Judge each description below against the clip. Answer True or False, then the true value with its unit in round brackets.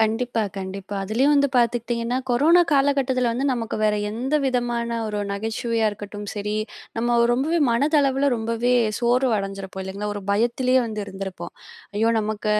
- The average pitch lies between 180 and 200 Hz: False (235 Hz)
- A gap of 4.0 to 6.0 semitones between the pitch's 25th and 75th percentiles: False (3.4 semitones)